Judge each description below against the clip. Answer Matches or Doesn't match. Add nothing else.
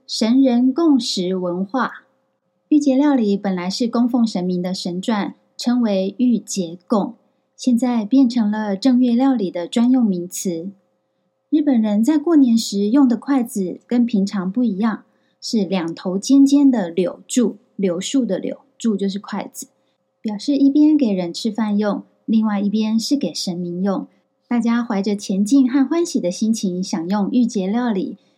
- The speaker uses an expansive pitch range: Doesn't match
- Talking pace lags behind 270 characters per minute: Matches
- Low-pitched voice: Doesn't match